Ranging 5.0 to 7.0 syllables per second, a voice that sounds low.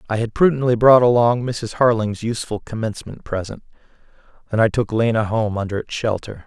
Yes: 5.7 syllables/s; low, 115 Hz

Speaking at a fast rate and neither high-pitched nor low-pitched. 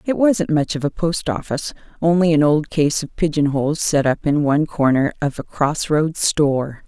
Yes: fast, 210 wpm; medium, 155 Hz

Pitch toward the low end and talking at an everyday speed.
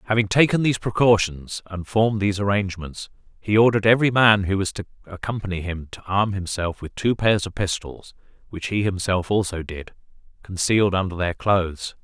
Yes: low, 100 Hz; average, 170 wpm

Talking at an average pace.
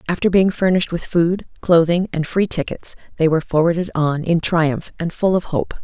Yes: average, 195 wpm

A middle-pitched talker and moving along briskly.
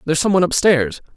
Yes: medium, 160 Hz; fast, 260 wpm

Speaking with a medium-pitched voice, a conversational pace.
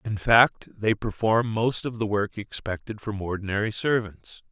No: low, 105 Hz; average, 160 wpm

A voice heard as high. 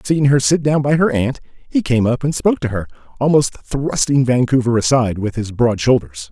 No: low, 130 Hz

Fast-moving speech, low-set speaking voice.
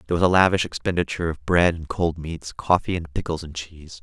Yes: fast, 225 wpm; very low, 85 Hz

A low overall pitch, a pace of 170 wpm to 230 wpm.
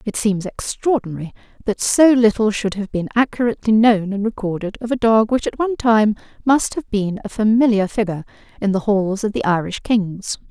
No: high, 215 Hz; average, 190 wpm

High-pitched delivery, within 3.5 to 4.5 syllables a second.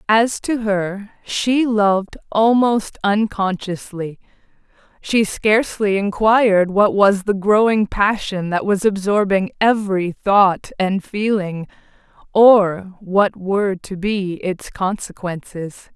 Yes: high, 200 Hz; 3.6 syllables/s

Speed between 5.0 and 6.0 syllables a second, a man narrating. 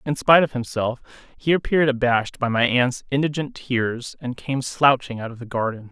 Yes: 5.2 syllables/s; male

